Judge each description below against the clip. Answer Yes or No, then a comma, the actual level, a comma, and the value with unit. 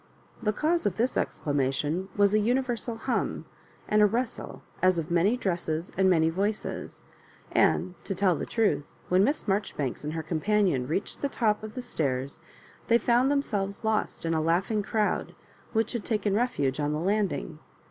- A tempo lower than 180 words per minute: Yes, average, 170 wpm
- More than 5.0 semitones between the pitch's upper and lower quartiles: Yes, wide, 5.4 semitones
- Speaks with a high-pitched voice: Yes, high, 200 Hz